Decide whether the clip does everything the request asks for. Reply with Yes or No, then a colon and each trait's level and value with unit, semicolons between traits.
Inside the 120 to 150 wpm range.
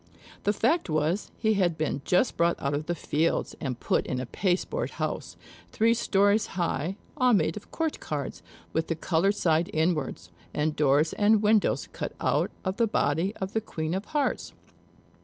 No: average, 175 wpm